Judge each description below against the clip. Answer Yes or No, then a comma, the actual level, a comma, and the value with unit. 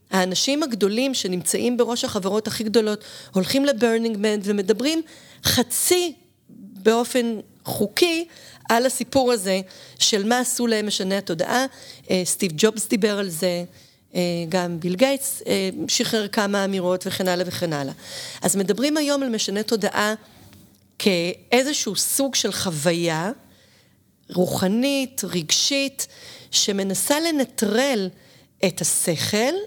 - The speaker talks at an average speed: Yes, average, 110 wpm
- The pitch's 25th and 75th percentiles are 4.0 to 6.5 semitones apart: Yes, average, 4.9 semitones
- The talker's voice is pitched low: No, high, 215 Hz